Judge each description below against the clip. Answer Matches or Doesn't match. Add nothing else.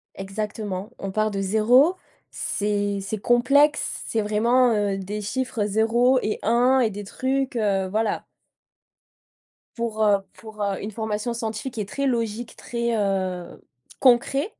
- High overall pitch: Matches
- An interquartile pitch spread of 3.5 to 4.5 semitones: Doesn't match